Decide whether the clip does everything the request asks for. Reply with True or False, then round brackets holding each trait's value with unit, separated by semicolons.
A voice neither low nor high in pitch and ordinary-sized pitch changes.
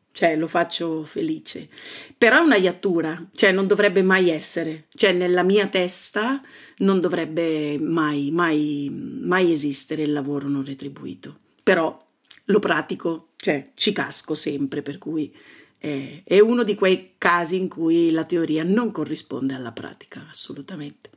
True (170 Hz; 4.2 semitones)